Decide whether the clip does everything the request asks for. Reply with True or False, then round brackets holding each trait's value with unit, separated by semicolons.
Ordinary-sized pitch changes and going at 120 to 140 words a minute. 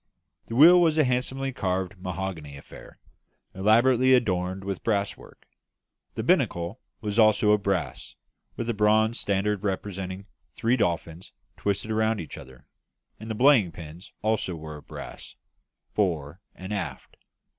True (3.6 semitones; 135 wpm)